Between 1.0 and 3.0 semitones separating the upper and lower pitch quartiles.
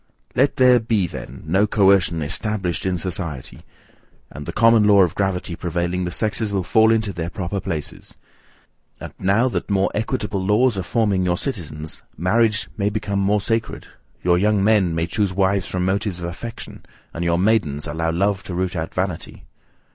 No: average, 3.4 semitones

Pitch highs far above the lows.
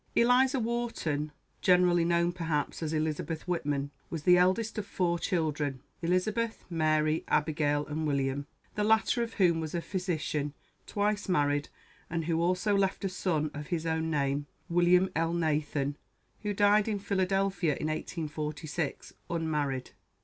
No: average, 3.9 semitones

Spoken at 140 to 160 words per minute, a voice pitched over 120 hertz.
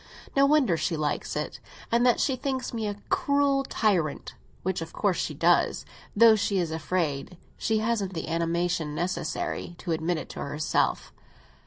Yes: average, 155 wpm; medium, 185 Hz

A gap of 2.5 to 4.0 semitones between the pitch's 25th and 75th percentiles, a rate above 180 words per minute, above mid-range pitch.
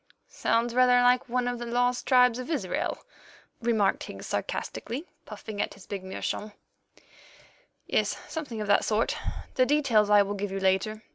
No: average, 3.3 semitones; average, 160 wpm; high, 230 Hz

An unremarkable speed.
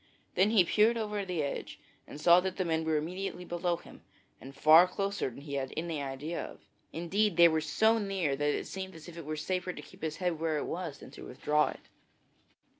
No: fast, 225 wpm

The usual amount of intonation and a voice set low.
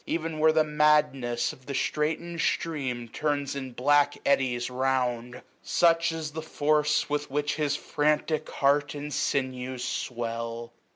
No: average, 3.0 semitones; medium, 145 Hz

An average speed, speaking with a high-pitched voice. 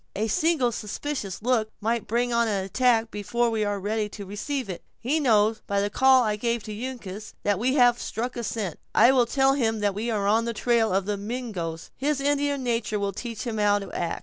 No: fast, 225 wpm; high, 225 Hz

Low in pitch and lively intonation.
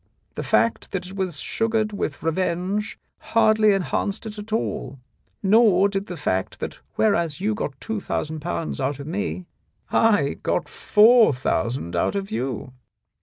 No: high, 190 Hz; wide, 6.0 semitones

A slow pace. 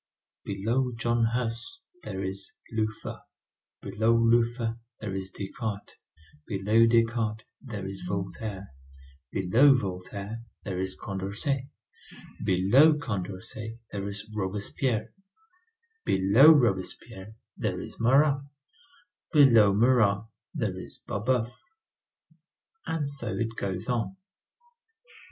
Yes: slow, 95 wpm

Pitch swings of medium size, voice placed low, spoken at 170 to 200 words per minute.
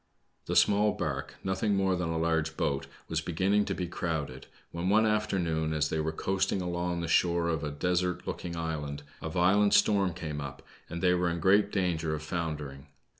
Yes: average, 3.1 semitones; very low, 85 Hz; average, 190 wpm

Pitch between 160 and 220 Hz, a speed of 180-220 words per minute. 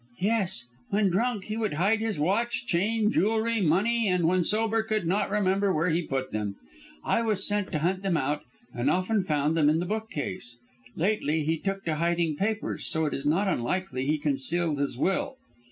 Yes: medium, 185 Hz; average, 190 wpm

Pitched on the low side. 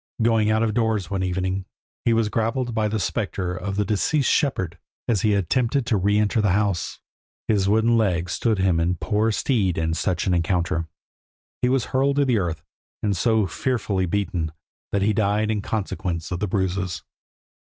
Yes: low, 105 Hz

